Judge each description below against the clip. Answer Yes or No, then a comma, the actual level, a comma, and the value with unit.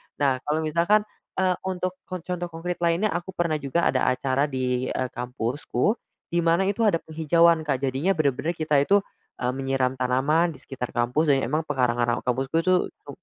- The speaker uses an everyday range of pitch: Yes, average, 4.7 semitones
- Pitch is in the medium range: Yes, medium, 150 Hz